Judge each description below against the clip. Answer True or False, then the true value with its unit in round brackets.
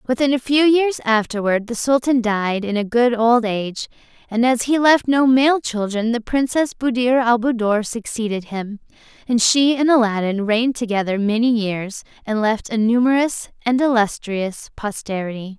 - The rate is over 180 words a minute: False (160 wpm)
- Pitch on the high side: True (235 Hz)